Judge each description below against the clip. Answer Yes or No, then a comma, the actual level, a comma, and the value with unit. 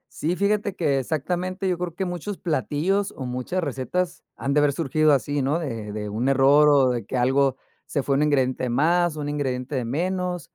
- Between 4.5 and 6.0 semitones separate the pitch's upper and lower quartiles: Yes, average, 5.0 semitones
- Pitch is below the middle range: No, medium, 145 Hz